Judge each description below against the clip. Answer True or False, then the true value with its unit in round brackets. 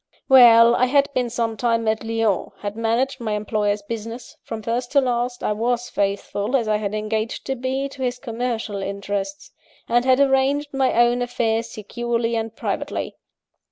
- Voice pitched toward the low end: False (235 Hz)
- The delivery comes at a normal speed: True (170 wpm)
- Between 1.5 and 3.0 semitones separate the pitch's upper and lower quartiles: True (2.6 semitones)